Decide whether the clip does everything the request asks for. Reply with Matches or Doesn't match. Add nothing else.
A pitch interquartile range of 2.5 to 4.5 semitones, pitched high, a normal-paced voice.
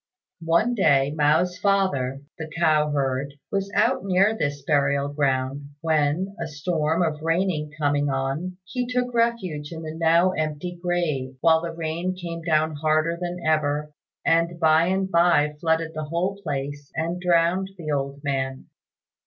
Doesn't match